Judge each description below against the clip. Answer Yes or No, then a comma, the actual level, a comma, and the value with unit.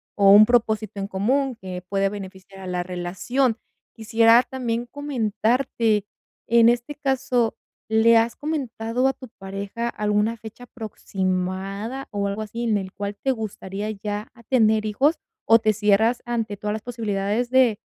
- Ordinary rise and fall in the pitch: Yes, average, 3.0 semitones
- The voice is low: No, high, 220 Hz